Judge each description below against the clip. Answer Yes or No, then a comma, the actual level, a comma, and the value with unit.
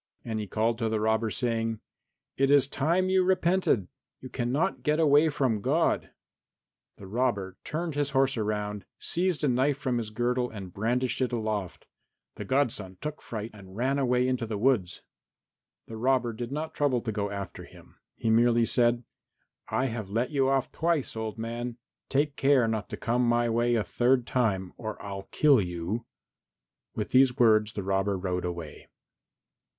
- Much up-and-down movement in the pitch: No, average, 3.8 semitones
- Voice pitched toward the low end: Yes, low, 120 Hz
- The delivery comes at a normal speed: Yes, average, 170 wpm